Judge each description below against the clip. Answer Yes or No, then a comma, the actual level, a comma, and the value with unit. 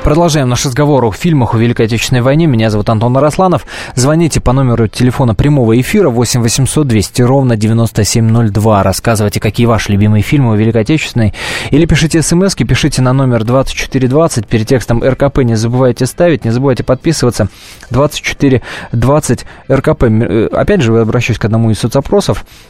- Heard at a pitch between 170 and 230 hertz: No, low, 125 Hz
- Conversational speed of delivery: Yes, average, 150 wpm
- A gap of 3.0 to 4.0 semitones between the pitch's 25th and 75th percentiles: Yes, average, 3.6 semitones